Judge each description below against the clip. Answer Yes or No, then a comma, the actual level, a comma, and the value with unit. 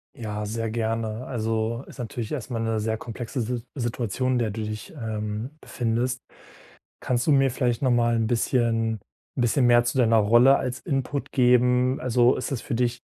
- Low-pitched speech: Yes, low, 120 Hz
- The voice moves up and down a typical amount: No, narrow, 2.0 semitones